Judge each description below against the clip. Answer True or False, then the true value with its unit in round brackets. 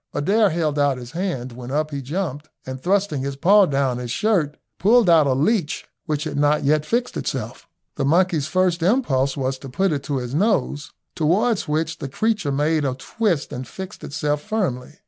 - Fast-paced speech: False (190 wpm)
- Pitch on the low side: False (150 Hz)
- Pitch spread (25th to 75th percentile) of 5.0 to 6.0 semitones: True (5.4 semitones)